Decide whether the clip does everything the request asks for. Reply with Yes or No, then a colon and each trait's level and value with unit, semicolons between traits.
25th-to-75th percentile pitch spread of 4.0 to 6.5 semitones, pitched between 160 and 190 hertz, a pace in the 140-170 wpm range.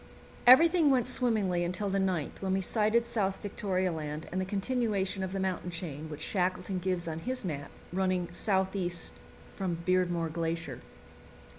No: average, 2.8 semitones; medium, 185 Hz; average, 155 wpm